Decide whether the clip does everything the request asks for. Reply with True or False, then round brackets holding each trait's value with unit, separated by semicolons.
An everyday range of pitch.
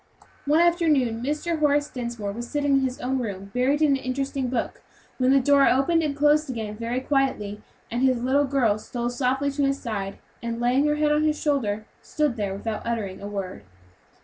True (3.8 semitones)